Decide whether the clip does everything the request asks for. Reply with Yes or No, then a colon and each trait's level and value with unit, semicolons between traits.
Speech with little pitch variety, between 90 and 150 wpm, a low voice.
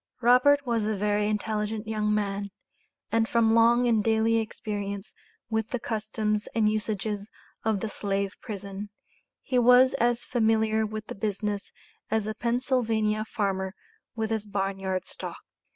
No: narrow, 1.6 semitones; average, 145 wpm; high, 215 Hz